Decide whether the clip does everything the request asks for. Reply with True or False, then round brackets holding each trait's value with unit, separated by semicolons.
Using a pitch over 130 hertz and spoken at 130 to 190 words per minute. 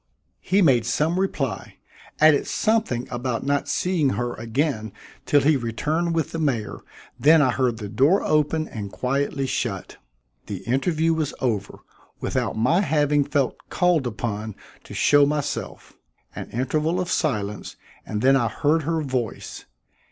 True (140 Hz; 145 wpm)